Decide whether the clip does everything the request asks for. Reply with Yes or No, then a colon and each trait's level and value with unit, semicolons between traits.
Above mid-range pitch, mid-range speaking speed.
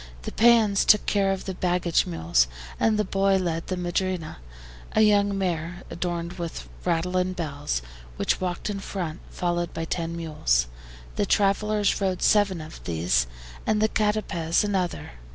No: medium, 180 Hz; average, 155 wpm